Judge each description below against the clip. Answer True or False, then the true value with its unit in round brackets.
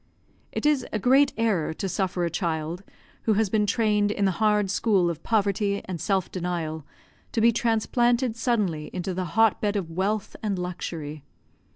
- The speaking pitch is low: False (200 Hz)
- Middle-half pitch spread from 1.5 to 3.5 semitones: False (4.0 semitones)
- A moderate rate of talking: True (175 wpm)